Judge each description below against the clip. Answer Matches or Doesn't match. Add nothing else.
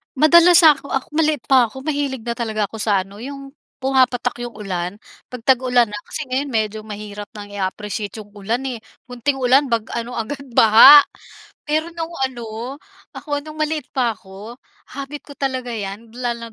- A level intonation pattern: Doesn't match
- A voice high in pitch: Matches